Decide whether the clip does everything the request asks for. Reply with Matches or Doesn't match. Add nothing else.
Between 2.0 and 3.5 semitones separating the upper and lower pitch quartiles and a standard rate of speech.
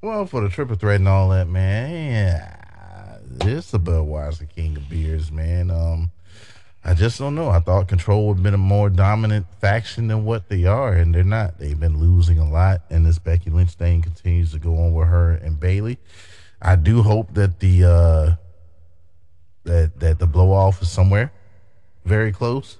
Matches